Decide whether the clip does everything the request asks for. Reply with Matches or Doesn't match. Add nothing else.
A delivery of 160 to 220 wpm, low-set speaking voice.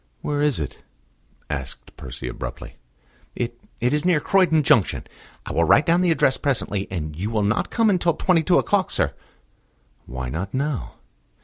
Matches